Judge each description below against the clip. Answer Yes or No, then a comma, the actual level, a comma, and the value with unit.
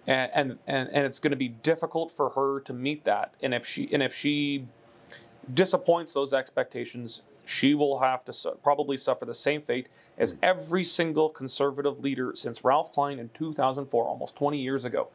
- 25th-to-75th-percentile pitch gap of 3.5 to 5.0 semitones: No, average, 2.7 semitones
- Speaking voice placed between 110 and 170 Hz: Yes, medium, 140 Hz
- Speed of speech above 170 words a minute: Yes, average, 180 wpm